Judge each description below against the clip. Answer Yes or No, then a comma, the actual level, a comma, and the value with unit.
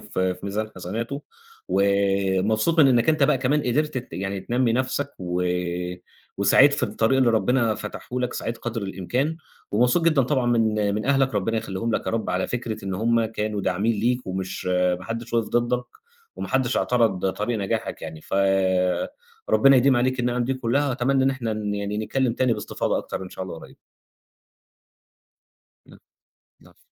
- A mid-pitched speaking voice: No, low, 115 Hz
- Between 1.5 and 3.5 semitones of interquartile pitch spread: No, average, 4.3 semitones